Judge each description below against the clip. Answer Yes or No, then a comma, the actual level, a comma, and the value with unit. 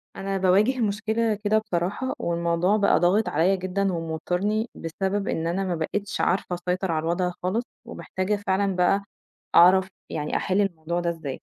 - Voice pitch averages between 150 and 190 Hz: Yes, medium, 185 Hz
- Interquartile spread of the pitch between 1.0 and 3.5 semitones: Yes, average, 2.9 semitones